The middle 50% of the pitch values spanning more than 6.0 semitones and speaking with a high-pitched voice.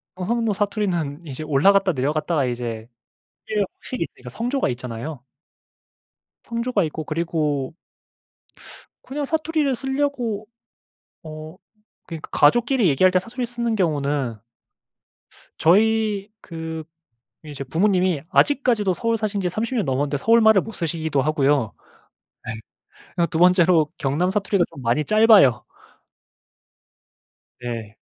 No: wide, 7.0 semitones; medium, 175 Hz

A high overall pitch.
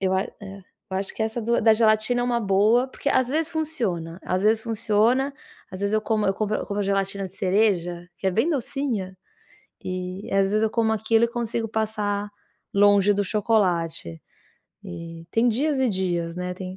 Yes: high, 210 Hz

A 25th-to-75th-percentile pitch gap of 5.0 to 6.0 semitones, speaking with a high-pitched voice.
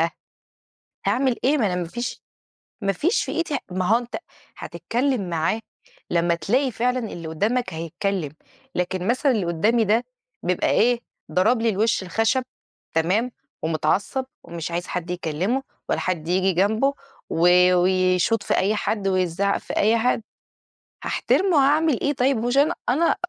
Yes: wide, 5.6 semitones; high, 210 Hz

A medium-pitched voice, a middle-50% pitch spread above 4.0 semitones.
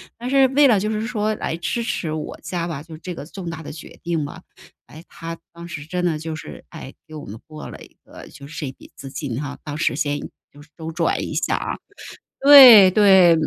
Yes: medium, 165 Hz; average, 4.4 semitones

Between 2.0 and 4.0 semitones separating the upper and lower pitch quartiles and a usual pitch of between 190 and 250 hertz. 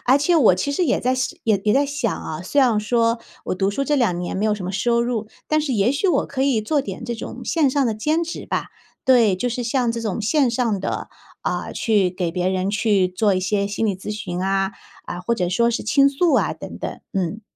No: wide, 5.5 semitones; high, 225 Hz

